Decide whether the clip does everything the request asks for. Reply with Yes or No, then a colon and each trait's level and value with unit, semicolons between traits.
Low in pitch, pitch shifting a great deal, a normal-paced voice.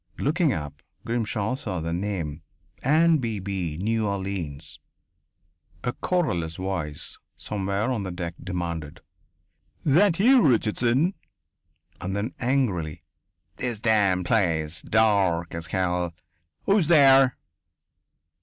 No: low, 100 Hz; wide, 6.7 semitones; slow, 105 wpm